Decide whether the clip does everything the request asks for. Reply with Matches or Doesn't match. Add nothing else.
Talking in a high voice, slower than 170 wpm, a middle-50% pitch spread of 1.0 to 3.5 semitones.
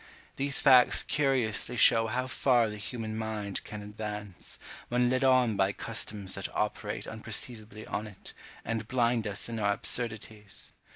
Doesn't match